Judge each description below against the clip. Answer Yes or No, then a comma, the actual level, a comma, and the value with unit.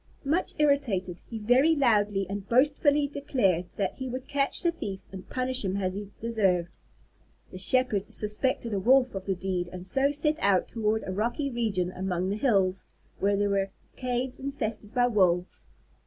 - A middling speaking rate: Yes, average, 170 wpm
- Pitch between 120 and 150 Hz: No, high, 215 Hz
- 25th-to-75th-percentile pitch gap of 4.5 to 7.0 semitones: Yes, average, 5.3 semitones